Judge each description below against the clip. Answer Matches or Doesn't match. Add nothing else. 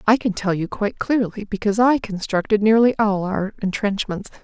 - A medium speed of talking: Matches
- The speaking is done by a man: Doesn't match